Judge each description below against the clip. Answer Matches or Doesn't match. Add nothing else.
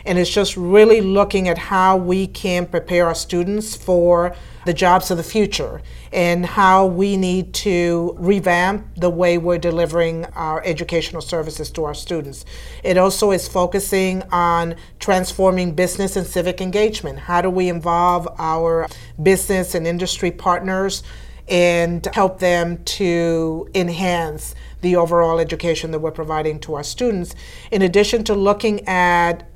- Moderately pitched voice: Matches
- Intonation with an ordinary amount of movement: Doesn't match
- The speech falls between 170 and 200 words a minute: Doesn't match